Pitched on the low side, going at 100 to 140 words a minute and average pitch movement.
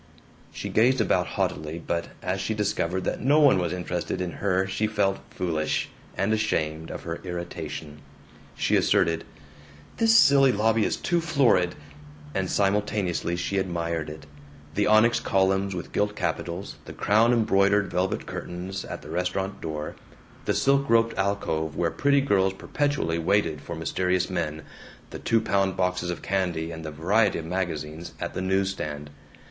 No: very low, 95 Hz; average, 160 wpm; average, 3.7 semitones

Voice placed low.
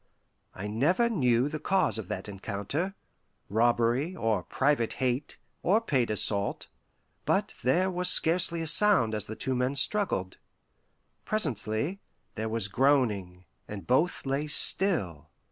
Yes: low, 130 Hz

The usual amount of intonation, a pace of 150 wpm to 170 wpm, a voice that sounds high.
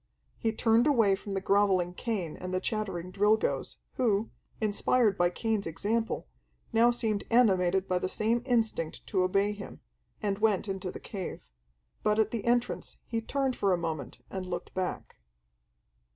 Yes: average, 3.5 semitones; average, 160 wpm; high, 205 Hz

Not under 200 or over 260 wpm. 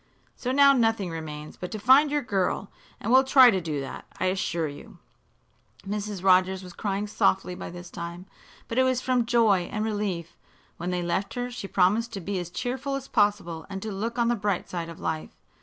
Yes: fast, 205 wpm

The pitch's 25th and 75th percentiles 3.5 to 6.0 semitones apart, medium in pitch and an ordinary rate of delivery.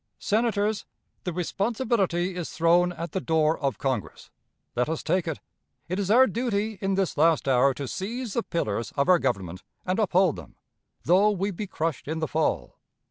Yes: average, 4.5 semitones; medium, 180 Hz; average, 180 wpm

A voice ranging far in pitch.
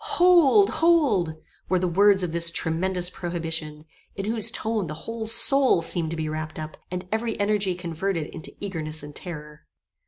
No: average, 5.0 semitones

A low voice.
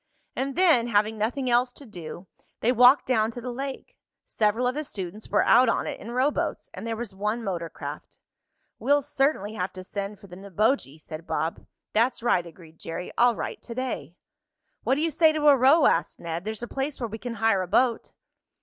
No: high, 230 Hz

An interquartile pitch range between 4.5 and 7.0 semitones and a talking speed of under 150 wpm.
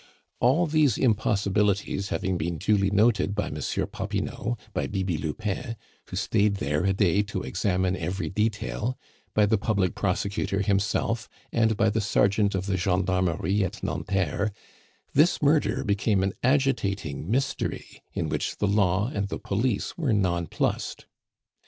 No: average, 2.7 semitones; average, 140 wpm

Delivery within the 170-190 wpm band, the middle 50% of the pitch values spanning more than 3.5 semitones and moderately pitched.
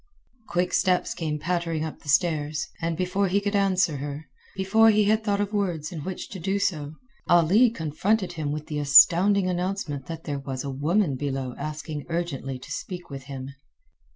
Yes: average, 180 wpm; average, 4.7 semitones; medium, 165 Hz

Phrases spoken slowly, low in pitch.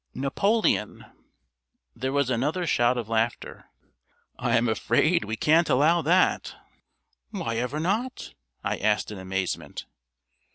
Yes: slow, 120 wpm; low, 130 Hz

